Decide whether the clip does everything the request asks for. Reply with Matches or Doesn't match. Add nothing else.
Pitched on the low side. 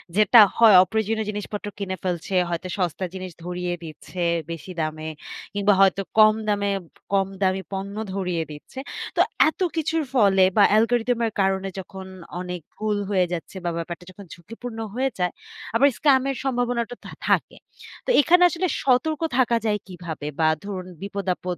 Doesn't match